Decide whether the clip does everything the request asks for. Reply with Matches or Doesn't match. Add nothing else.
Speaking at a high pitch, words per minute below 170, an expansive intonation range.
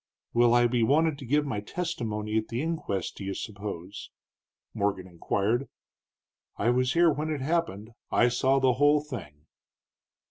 Doesn't match